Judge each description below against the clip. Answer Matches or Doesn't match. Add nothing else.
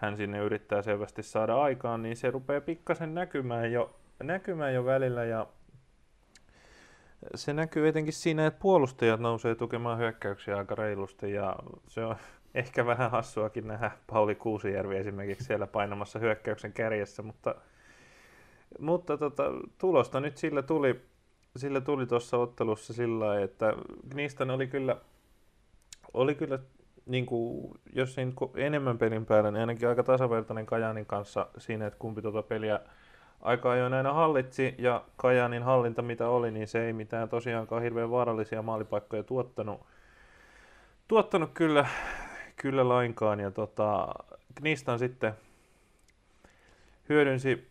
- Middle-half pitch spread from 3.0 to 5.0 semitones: Matches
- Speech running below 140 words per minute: Matches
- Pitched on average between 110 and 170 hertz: Matches